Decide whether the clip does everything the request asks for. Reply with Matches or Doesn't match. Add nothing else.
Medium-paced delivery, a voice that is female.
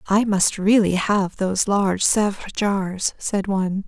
Matches